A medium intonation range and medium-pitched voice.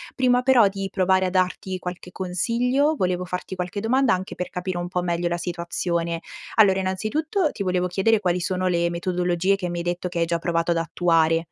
No: narrow, 2.0 semitones; medium, 180 Hz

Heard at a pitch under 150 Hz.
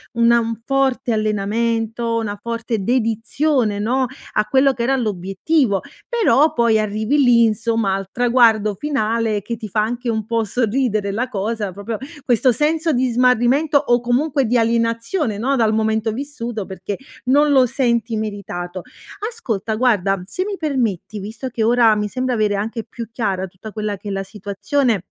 No: high, 230 Hz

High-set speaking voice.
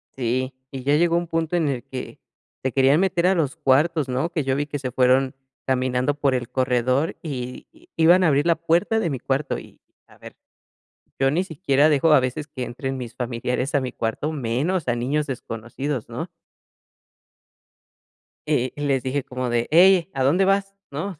No: medium, 140 Hz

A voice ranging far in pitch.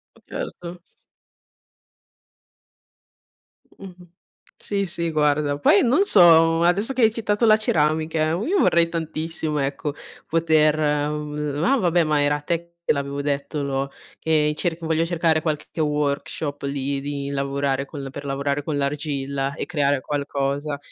No: average, 2.9 semitones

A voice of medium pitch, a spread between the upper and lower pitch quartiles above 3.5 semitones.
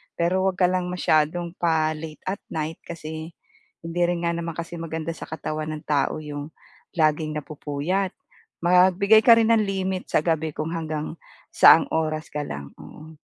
No: medium, 160 Hz; narrow, 2.4 semitones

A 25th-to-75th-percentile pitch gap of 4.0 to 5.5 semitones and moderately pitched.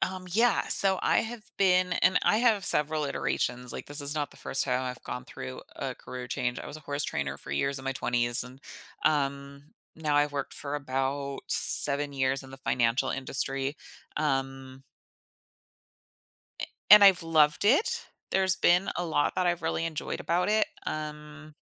Yes: average, 4.6 semitones; medium, 145 Hz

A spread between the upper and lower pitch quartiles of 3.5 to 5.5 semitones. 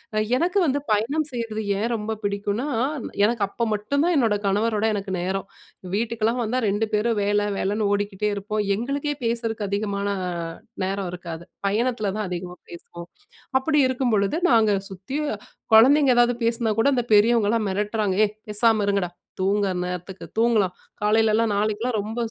No: average, 2.7 semitones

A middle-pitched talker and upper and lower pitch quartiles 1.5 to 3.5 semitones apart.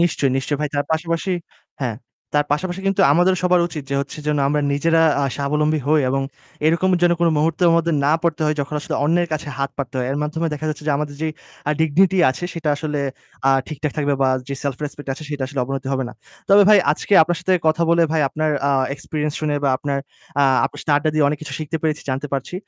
Yes: medium, 150 Hz; narrow, 2.6 semitones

